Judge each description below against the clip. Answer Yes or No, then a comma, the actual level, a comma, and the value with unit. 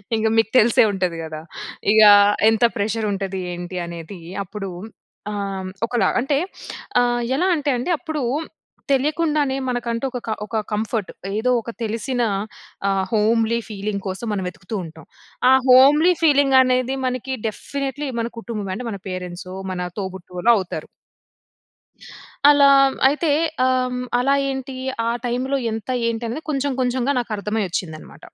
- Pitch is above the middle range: Yes, high, 230 Hz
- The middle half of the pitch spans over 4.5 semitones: Yes, average, 5.1 semitones